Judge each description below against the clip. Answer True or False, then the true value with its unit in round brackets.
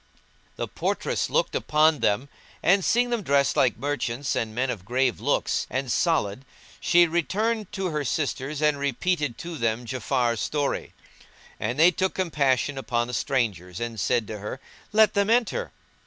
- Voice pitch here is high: False (140 Hz)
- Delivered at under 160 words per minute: False (165 wpm)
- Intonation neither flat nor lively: False (6.3 semitones)